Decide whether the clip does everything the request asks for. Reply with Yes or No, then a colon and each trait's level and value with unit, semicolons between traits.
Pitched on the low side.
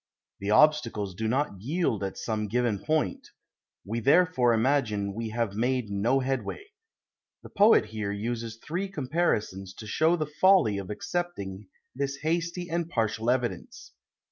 Yes: low, 120 Hz